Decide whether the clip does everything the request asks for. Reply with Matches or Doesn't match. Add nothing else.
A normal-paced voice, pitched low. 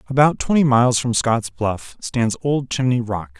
Matches